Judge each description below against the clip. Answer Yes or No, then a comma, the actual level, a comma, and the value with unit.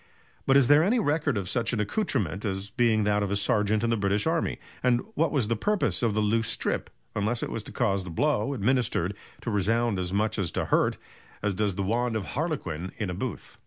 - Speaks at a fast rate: Yes, fast, 230 wpm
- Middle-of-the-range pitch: No, low, 110 Hz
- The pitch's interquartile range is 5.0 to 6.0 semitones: No, average, 3.9 semitones